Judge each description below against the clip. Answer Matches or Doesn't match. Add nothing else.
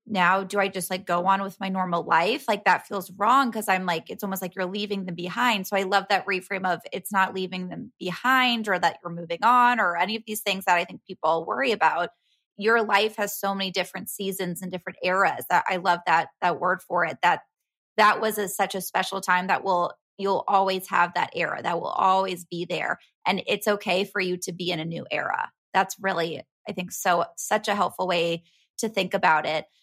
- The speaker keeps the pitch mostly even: Matches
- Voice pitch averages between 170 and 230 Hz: Matches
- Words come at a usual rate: Doesn't match